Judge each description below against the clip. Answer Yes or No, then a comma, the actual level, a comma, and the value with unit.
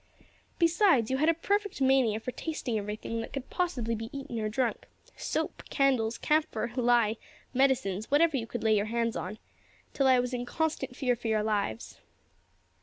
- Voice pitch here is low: No, high, 245 Hz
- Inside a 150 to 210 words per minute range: Yes, average, 175 wpm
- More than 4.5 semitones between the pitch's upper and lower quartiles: No, average, 3.8 semitones